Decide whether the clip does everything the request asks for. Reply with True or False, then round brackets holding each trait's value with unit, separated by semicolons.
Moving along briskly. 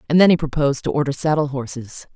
True (225 wpm)